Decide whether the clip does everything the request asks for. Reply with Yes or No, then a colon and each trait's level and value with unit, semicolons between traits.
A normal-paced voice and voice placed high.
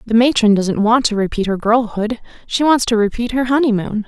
Yes: average, 190 wpm; high, 225 Hz